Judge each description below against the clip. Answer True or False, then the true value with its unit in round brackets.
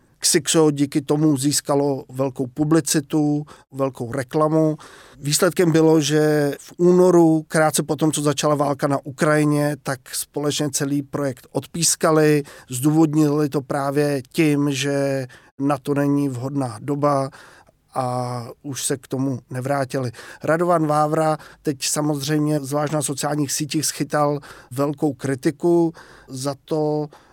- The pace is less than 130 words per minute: True (120 wpm)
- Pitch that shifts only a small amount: True (1.8 semitones)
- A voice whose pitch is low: False (145 Hz)